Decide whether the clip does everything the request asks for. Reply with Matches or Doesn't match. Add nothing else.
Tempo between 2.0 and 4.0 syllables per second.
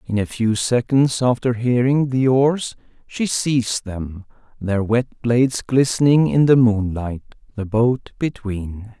Matches